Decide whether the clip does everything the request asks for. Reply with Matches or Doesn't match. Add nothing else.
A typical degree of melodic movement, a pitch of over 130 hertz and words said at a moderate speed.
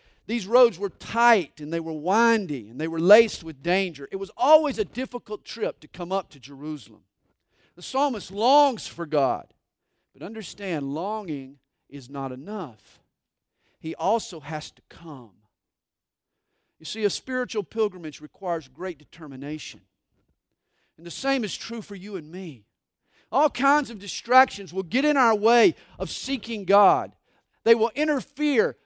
Doesn't match